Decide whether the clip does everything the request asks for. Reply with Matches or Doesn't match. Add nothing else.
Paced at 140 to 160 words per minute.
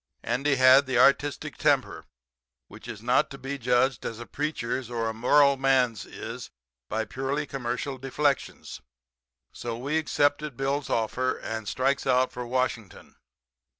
Matches